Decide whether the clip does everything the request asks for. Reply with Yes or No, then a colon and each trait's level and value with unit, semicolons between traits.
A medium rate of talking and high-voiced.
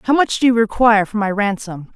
No: fast, 245 wpm; high, 215 Hz